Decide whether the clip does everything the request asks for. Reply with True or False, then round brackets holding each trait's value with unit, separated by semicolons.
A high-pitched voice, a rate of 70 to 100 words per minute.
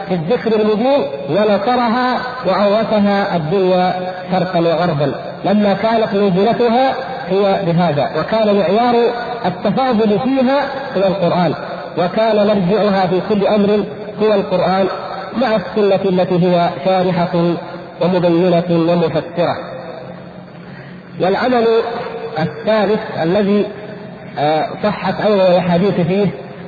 True (195 Hz; 90 wpm)